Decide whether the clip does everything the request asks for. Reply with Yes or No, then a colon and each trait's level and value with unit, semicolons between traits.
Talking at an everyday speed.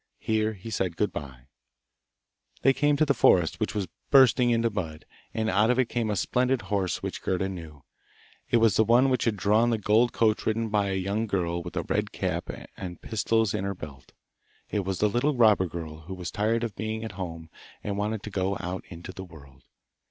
No: fast, 215 wpm